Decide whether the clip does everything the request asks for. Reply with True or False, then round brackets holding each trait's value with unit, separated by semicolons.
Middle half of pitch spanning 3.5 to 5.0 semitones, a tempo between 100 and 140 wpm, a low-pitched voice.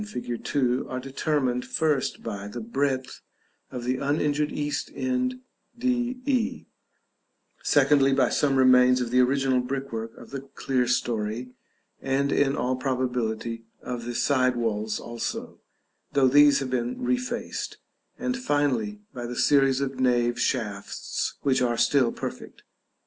False (2.8 semitones; 135 wpm; 130 Hz)